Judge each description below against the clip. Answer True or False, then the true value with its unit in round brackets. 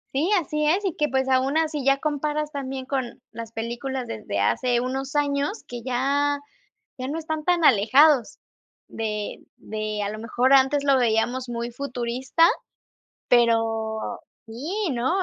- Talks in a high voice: True (265 Hz)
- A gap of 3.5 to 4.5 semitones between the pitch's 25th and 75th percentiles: True (3.8 semitones)